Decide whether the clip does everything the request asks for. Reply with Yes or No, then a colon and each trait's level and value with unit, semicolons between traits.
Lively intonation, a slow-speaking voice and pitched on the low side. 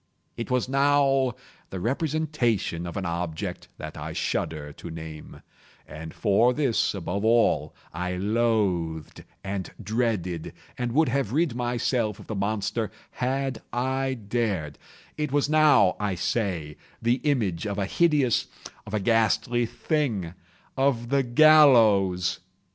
Yes: wide, 6.2 semitones; slow, 120 wpm; low, 115 Hz